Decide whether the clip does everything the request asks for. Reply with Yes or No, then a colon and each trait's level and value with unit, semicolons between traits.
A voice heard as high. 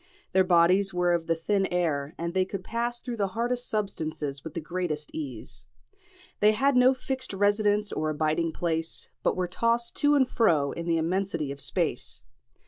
No: medium, 180 Hz